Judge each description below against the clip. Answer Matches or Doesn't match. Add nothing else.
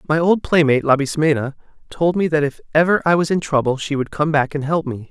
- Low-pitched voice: Doesn't match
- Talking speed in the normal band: Doesn't match